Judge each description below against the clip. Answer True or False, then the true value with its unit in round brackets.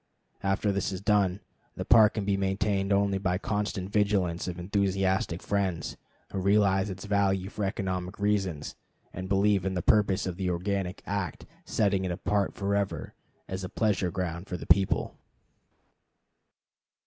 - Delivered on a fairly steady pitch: True (1.5 semitones)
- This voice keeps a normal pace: True (155 wpm)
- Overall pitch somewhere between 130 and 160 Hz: False (95 Hz)